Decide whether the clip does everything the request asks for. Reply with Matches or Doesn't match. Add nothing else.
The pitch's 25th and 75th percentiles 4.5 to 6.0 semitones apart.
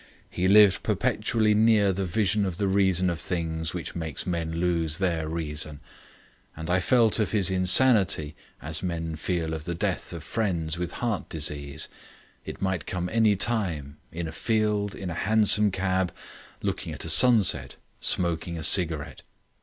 Doesn't match